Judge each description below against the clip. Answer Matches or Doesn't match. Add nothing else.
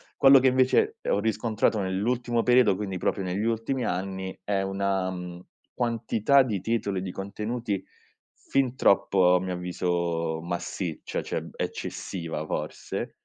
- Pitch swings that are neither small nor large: Matches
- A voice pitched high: Doesn't match